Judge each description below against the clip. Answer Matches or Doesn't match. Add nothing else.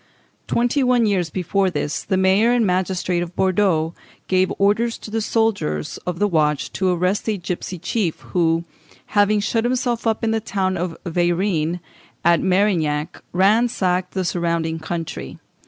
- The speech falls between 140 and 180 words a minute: Matches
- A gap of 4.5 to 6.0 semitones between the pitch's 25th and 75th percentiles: Doesn't match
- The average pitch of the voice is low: Doesn't match